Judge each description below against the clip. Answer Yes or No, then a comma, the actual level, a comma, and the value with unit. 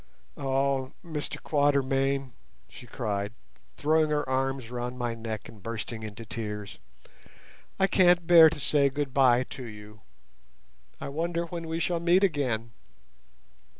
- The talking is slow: Yes, slow, 130 wpm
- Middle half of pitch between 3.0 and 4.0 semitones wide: No, average, 5.1 semitones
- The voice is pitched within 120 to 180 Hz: Yes, low, 135 Hz